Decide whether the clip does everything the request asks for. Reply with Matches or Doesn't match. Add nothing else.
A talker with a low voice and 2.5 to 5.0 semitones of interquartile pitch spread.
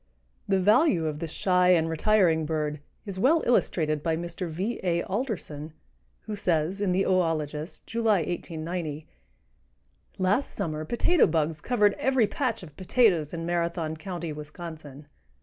Doesn't match